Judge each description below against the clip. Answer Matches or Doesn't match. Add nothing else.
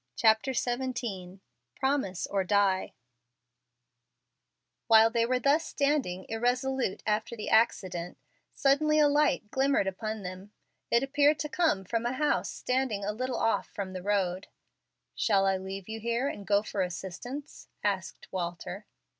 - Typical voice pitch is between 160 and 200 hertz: Doesn't match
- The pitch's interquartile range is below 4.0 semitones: Doesn't match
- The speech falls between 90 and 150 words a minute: Matches